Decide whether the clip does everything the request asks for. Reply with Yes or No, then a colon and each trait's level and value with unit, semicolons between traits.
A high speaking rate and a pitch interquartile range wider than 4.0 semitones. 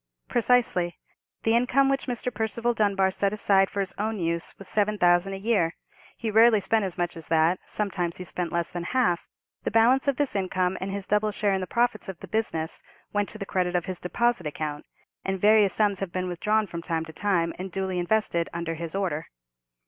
No: fast, 210 wpm; average, 3.7 semitones